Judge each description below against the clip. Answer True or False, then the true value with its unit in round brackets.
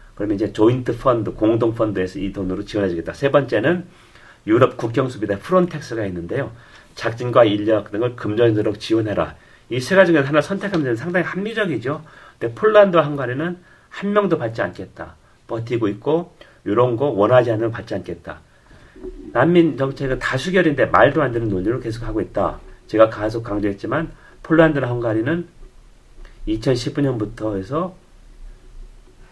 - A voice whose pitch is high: False (125 Hz)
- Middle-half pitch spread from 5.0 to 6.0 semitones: False (6.9 semitones)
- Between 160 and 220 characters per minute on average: False (340 characters per minute)